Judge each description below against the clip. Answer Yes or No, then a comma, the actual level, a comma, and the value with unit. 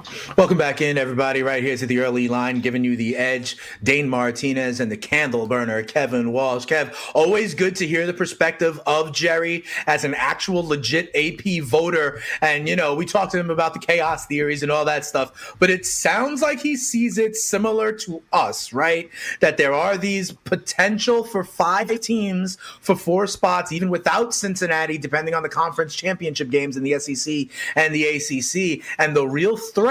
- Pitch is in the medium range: Yes, medium, 160 Hz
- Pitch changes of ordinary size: Yes, average, 4.6 semitones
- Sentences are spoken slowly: No, average, 185 wpm